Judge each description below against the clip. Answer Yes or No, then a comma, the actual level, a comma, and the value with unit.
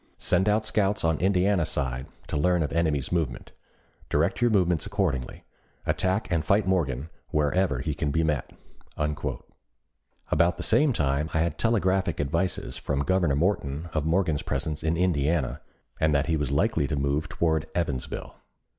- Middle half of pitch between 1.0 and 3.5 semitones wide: No, average, 4.2 semitones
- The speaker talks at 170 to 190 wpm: No, average, 155 wpm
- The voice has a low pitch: Yes, very low, 80 Hz